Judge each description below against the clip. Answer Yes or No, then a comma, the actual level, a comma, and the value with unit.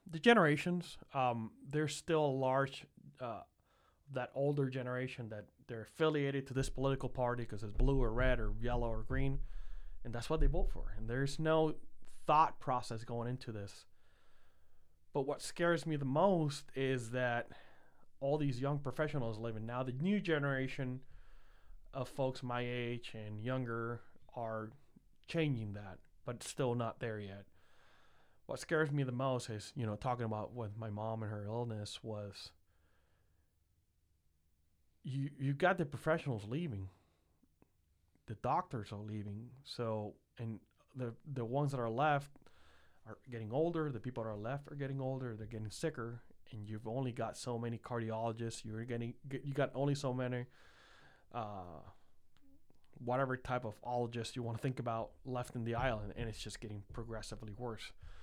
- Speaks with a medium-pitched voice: No, low, 120 Hz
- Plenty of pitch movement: No, average, 4.2 semitones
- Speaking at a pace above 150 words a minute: Yes, average, 160 wpm